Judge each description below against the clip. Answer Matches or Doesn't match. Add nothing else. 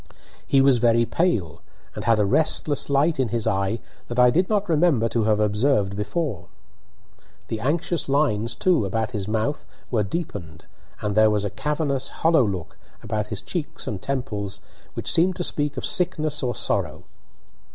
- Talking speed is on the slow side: Doesn't match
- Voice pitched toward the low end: Matches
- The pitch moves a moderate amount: Doesn't match